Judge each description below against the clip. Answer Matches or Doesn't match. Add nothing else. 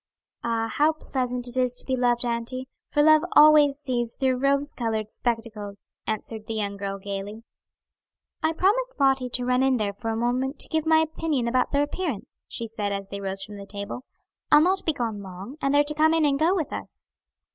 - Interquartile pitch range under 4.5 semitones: Doesn't match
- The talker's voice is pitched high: Matches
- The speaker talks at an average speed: Doesn't match